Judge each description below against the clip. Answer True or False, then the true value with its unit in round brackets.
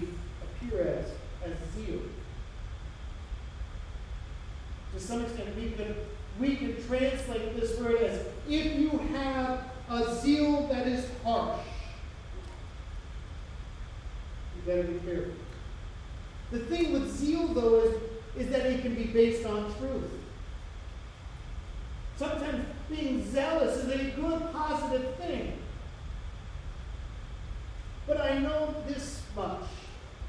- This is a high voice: True (225 Hz)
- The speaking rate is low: True (105 wpm)